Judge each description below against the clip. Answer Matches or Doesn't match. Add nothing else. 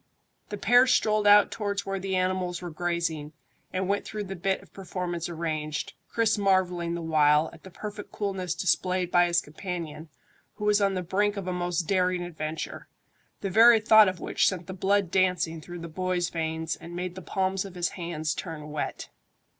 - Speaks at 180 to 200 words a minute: Matches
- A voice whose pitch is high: Doesn't match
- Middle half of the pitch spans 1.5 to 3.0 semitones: Matches